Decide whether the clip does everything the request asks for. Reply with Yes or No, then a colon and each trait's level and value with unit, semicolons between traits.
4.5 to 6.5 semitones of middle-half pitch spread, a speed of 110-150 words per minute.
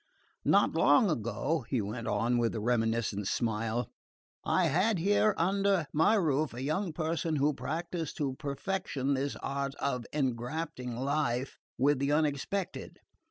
Yes: average, 5.1 semitones; average, 140 wpm